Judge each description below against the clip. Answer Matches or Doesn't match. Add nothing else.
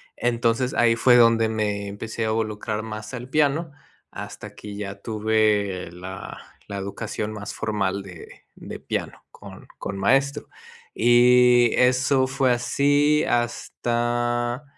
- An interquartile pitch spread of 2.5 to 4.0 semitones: Matches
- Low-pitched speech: Matches